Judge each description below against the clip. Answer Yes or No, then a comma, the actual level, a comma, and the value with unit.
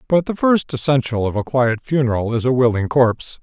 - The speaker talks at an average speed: No, fast, 210 wpm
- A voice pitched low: Yes, low, 130 Hz